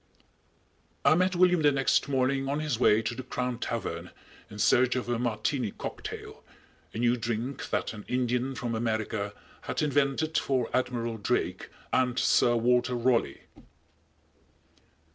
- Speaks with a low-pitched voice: Yes, low, 125 Hz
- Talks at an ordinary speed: Yes, average, 145 wpm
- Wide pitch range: No, average, 2.7 semitones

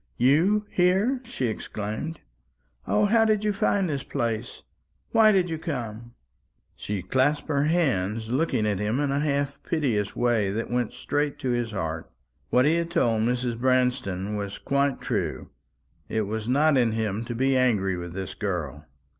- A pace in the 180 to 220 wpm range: No, average, 165 wpm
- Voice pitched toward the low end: Yes, low, 125 Hz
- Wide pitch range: Yes, wide, 6.1 semitones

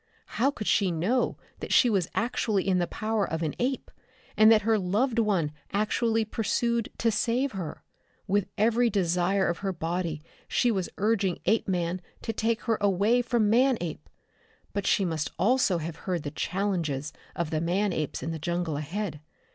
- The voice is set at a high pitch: Yes, high, 200 Hz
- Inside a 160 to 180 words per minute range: Yes, average, 170 wpm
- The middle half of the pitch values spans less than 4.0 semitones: No, average, 4.6 semitones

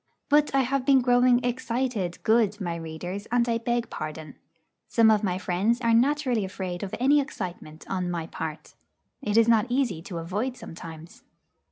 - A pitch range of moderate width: No, wide, 5.7 semitones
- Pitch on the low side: No, high, 220 Hz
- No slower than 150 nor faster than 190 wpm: Yes, average, 170 wpm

